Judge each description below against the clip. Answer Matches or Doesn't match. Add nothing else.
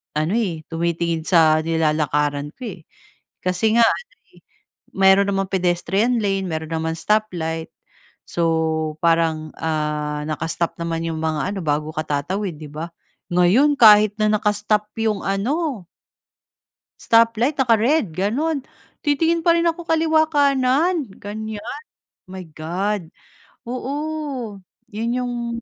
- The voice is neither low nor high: Doesn't match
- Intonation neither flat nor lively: Doesn't match